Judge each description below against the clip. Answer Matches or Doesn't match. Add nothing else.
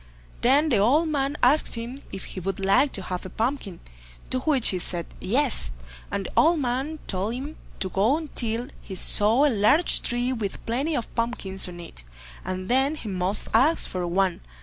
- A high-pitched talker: Matches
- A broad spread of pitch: Matches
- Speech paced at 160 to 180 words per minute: Doesn't match